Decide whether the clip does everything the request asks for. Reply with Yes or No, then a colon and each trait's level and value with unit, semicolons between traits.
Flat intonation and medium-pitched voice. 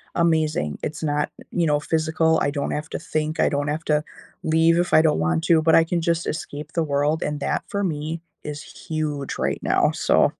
Yes: narrow, 1.6 semitones; medium, 155 Hz